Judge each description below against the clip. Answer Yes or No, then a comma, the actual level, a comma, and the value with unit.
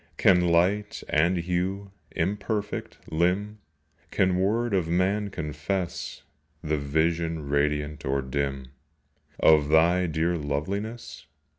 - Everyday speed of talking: No, slow, 105 wpm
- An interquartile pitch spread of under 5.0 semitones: Yes, average, 4.2 semitones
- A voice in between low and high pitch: No, very low, 85 Hz